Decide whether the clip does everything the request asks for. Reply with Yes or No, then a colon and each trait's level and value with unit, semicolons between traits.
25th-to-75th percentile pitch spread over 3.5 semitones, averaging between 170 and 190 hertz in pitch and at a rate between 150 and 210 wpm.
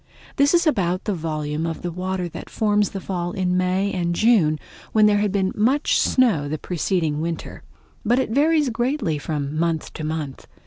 Yes: average, 5.1 semitones; medium, 185 Hz; average, 180 wpm